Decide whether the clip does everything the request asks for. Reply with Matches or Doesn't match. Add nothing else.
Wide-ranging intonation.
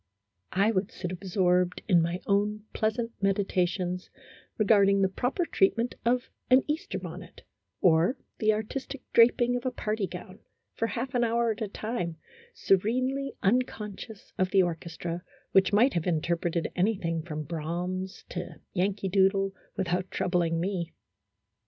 Doesn't match